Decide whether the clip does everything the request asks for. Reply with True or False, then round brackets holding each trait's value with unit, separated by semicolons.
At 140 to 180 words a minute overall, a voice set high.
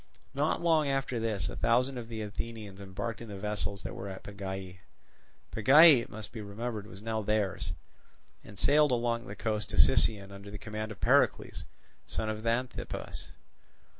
False (170 wpm; 110 Hz)